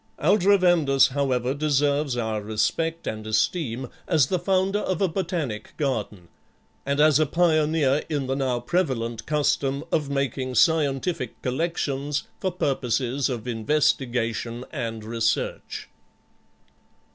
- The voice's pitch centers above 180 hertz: No, medium, 140 Hz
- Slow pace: Yes, slow, 115 wpm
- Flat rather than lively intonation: No, average, 4.7 semitones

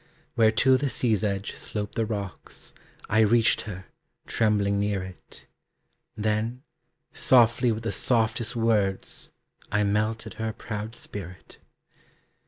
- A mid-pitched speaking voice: No, low, 110 Hz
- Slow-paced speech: Yes, slow, 120 wpm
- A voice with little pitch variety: Yes, narrow, 1.9 semitones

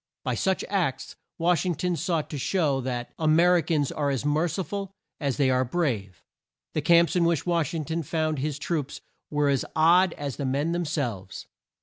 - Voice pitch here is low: No, medium, 155 Hz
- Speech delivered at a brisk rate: Yes, fast, 210 wpm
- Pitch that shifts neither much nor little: Yes, average, 3.6 semitones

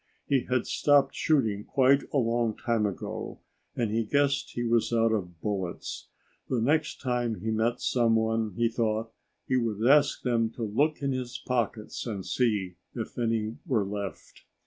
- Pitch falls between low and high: No, low, 115 Hz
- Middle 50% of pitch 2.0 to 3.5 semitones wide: Yes, average, 2.7 semitones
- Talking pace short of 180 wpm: Yes, average, 165 wpm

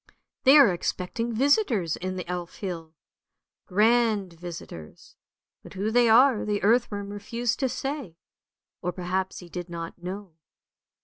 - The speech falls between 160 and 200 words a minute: No, slow, 135 wpm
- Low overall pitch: No, high, 200 Hz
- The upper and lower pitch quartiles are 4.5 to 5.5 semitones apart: Yes, average, 4.8 semitones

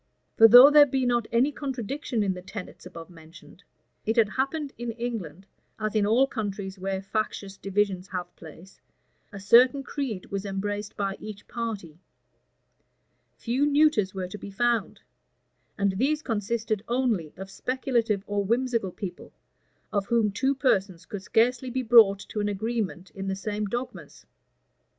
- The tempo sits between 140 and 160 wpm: Yes, average, 155 wpm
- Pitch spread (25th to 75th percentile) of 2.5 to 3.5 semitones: No, average, 3.9 semitones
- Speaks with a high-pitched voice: Yes, high, 210 Hz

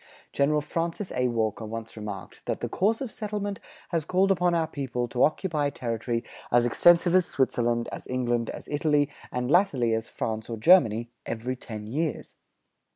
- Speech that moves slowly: No, average, 165 wpm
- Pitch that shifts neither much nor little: No, wide, 6.5 semitones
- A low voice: Yes, low, 130 Hz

